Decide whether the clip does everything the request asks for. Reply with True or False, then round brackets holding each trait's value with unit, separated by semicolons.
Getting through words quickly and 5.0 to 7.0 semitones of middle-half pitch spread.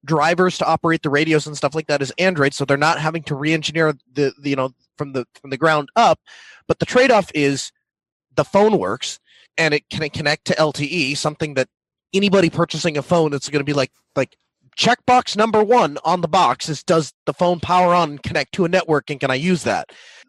False (225 wpm; 3.6 semitones)